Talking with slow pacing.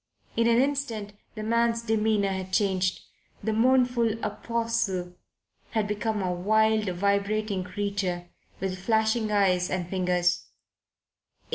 Yes: slow, 115 wpm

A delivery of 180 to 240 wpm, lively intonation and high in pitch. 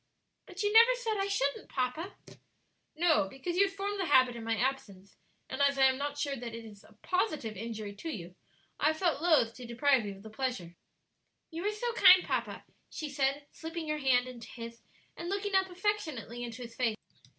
Yes: fast, 205 wpm; wide, 7.6 semitones; very high, 280 Hz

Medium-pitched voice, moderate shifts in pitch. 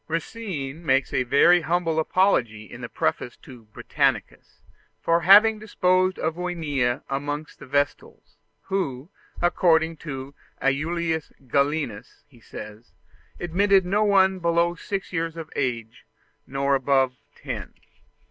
Yes: medium, 160 Hz; average, 4.8 semitones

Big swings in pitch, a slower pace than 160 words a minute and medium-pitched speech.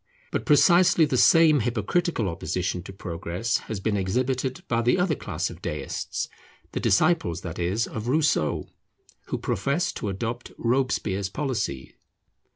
No: wide, 7.2 semitones; average, 140 wpm; low, 115 Hz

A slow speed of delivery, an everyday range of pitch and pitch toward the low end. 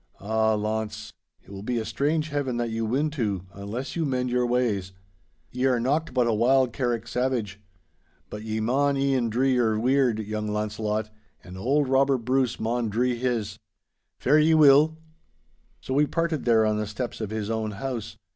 No: average, 180 wpm; average, 3.6 semitones; low, 120 Hz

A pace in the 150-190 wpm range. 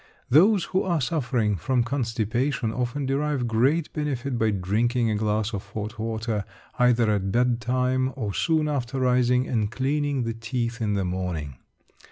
Yes: average, 155 wpm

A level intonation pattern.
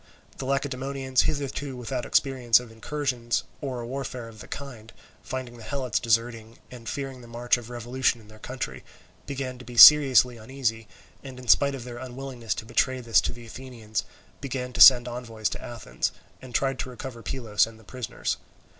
Yes: narrow, 2.3 semitones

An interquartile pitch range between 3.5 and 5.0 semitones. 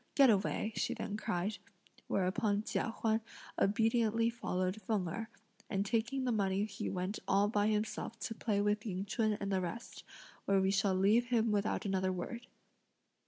No: narrow, 2.4 semitones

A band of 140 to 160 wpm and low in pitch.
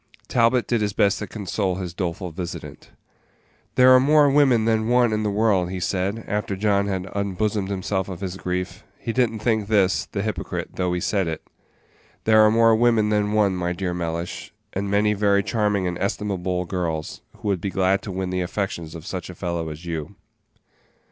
No: average, 195 wpm; low, 100 Hz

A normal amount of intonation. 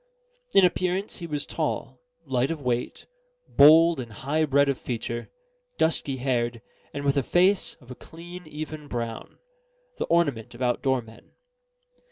Yes: average, 5.0 semitones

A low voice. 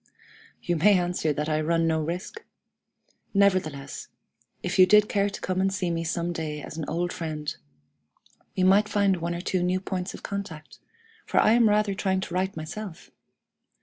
No: medium, 180 Hz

